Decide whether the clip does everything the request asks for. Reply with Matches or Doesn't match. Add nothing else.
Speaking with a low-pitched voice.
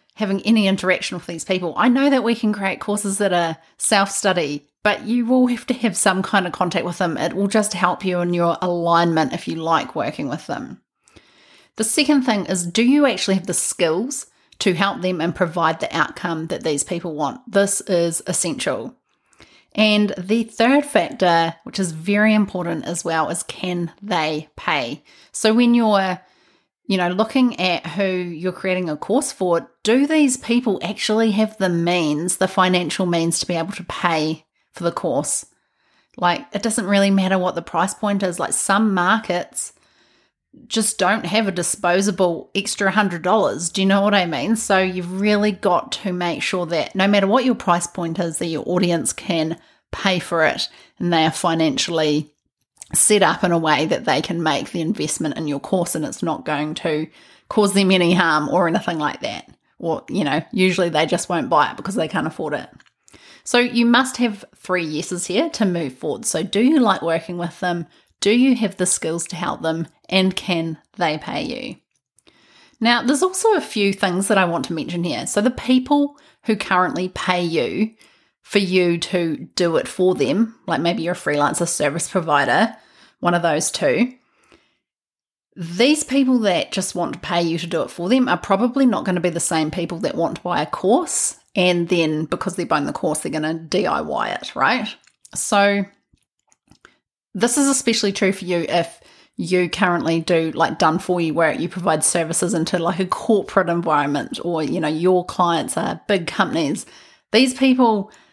Doesn't match